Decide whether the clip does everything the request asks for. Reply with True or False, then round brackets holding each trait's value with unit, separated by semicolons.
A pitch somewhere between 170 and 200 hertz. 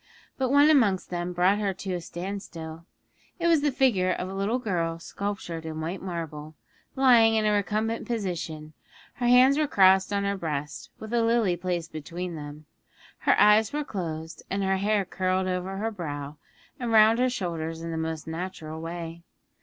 True (185 Hz)